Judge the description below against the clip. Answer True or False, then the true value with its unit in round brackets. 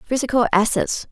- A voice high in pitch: True (240 Hz)